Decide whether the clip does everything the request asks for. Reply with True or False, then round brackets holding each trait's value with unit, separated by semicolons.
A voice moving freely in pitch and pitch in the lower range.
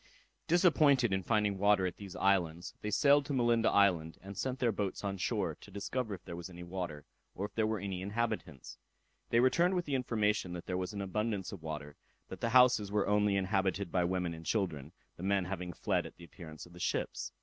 False (3.9 semitones; 100 Hz)